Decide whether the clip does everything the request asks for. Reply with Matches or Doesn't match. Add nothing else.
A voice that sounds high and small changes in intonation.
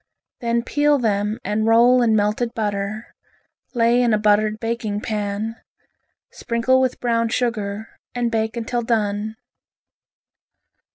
Matches